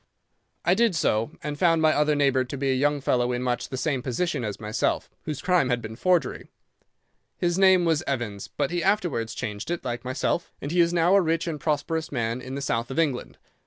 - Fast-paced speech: Yes, fast, 220 wpm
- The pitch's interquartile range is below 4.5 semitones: No, average, 5.2 semitones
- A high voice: No, medium, 145 Hz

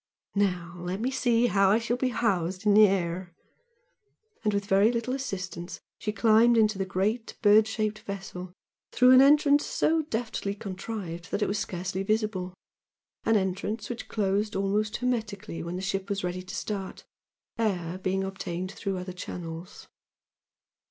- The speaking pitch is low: No, high, 200 Hz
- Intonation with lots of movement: No, average, 3.1 semitones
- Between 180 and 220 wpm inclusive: No, average, 155 wpm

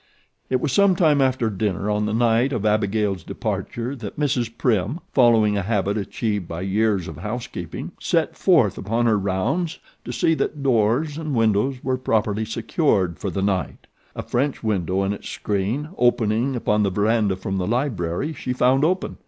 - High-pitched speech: No, low, 110 Hz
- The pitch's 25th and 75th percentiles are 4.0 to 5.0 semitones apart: Yes, average, 4.4 semitones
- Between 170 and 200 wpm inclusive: Yes, average, 175 wpm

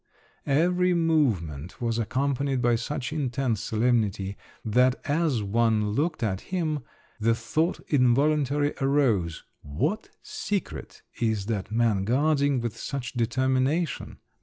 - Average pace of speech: No, slow, 110 wpm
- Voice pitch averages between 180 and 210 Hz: No, low, 125 Hz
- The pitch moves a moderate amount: Yes, average, 4.8 semitones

